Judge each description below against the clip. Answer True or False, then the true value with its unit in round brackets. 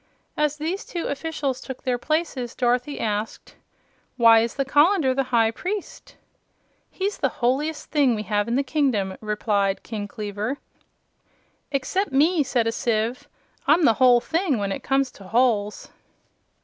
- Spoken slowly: False (150 wpm)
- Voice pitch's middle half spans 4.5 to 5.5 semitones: True (4.8 semitones)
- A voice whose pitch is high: True (255 Hz)